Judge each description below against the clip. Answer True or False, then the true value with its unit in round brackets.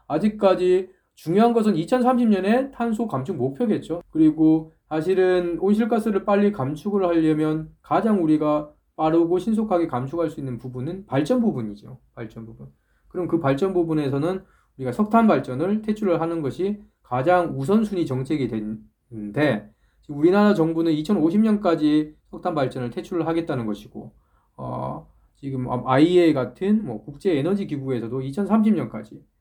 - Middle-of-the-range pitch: True (160 Hz)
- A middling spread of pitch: False (6.8 semitones)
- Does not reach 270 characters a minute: False (310 characters per minute)